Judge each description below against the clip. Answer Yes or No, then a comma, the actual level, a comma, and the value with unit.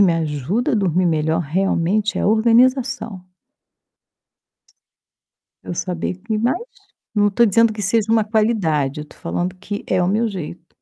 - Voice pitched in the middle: No, high, 195 Hz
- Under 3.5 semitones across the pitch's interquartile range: No, average, 4.3 semitones